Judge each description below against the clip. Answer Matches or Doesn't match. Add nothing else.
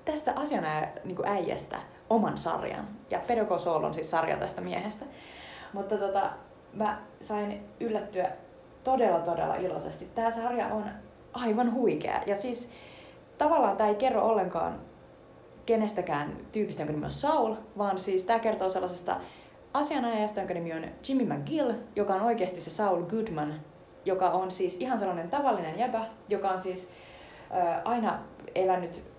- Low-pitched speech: Doesn't match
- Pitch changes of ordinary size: Matches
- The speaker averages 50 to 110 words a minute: Doesn't match